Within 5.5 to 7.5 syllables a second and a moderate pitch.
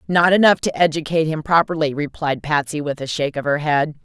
Yes: 6.0 syllables/s; medium, 155 Hz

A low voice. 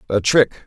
Yes: low, 115 Hz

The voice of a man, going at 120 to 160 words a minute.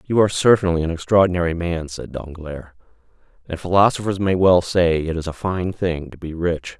No: male; average, 185 wpm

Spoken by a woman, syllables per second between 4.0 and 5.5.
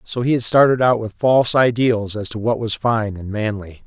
No: male; 5.1 syllables/s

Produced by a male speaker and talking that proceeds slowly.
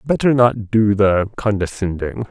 Yes: male; slow, 130 wpm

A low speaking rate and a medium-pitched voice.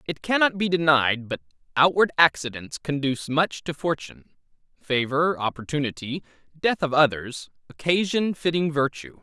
Yes: slow, 125 wpm; medium, 150 Hz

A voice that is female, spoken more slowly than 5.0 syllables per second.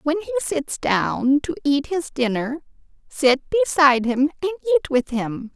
Yes: female; 4.6 syllables/s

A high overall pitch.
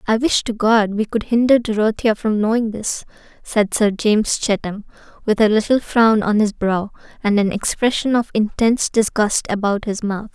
Yes: high, 215 Hz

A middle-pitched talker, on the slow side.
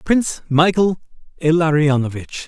Yes: medium, 160 Hz; slow, 75 wpm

